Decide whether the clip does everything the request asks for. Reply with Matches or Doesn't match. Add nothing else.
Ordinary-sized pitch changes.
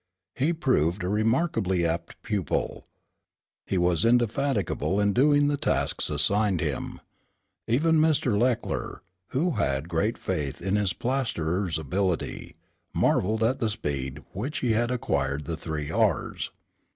Doesn't match